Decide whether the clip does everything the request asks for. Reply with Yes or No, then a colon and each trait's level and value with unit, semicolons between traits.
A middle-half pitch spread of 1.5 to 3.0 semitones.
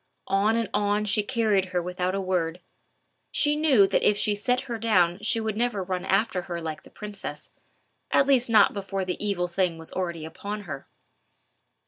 No: average, 3.4 semitones